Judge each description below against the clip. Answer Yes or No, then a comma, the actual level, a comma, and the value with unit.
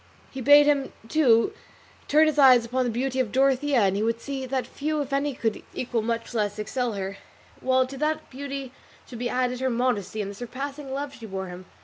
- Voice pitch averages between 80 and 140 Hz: No, very high, 255 Hz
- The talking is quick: Yes, fast, 215 wpm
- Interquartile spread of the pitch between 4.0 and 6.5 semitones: No, average, 3.2 semitones